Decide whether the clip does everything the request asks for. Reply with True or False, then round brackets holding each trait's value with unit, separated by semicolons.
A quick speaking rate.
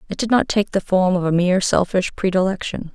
True (225 wpm)